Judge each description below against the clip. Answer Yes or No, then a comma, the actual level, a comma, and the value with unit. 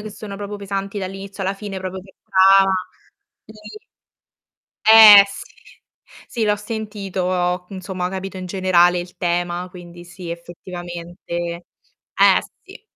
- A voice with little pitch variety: Yes, narrow, 2.1 semitones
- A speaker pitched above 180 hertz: Yes, high, 190 Hz